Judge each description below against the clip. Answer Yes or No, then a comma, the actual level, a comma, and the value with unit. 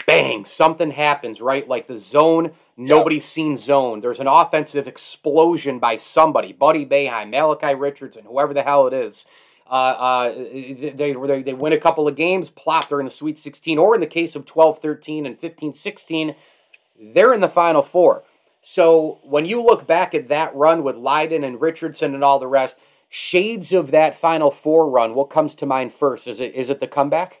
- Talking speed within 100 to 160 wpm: No, average, 195 wpm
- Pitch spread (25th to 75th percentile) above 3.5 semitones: No, narrow, 2.5 semitones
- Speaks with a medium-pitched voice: Yes, medium, 150 Hz